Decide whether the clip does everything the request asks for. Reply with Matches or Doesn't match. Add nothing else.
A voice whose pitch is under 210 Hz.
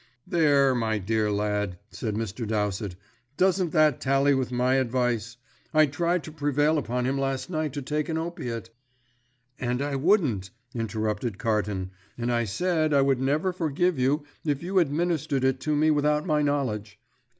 Matches